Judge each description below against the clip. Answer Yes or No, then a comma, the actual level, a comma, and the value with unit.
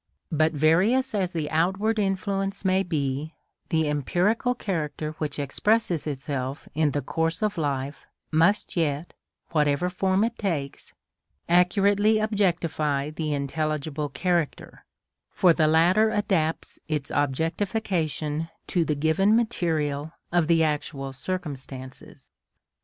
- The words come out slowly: Yes, slow, 115 wpm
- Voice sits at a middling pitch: Yes, medium, 160 Hz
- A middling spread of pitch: Yes, average, 4.6 semitones